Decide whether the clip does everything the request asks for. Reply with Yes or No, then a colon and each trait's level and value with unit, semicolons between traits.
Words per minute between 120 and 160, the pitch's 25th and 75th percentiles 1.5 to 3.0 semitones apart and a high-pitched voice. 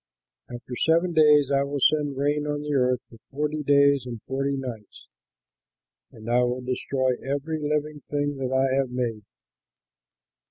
No: average, 155 wpm; narrow, 2.6 semitones; medium, 140 Hz